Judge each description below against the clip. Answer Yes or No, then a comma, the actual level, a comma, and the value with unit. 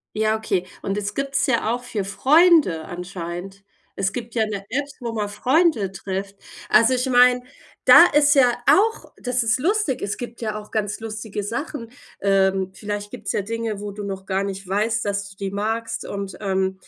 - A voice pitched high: Yes, high, 215 Hz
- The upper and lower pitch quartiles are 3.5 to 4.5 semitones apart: Yes, average, 3.9 semitones